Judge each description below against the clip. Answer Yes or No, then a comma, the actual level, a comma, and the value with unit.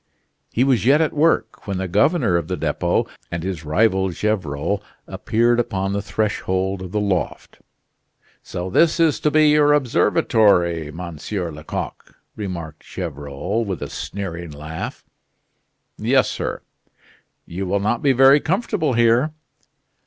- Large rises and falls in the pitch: Yes, wide, 5.8 semitones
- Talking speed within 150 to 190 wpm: No, average, 140 wpm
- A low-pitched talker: Yes, low, 100 Hz